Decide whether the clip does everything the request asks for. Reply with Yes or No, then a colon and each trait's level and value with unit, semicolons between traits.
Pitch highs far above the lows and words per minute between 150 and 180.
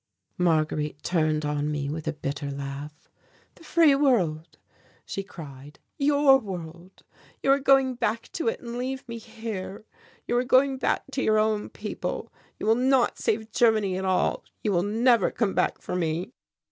Yes: wide, 7.8 semitones; average, 170 wpm